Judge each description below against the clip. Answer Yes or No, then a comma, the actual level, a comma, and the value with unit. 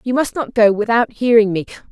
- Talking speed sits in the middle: No, fast, 220 wpm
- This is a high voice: Yes, high, 225 Hz